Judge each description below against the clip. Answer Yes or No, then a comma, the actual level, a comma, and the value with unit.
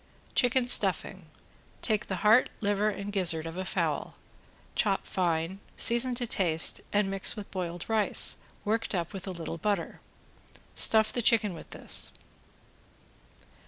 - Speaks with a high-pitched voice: Yes, high, 200 Hz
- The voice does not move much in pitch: No, average, 3.6 semitones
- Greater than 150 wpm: No, average, 140 wpm